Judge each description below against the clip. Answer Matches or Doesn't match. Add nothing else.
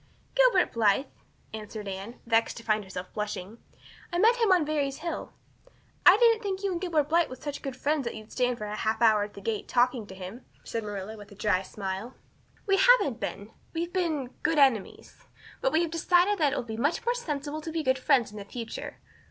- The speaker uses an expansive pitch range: Matches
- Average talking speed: Doesn't match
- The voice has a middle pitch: Doesn't match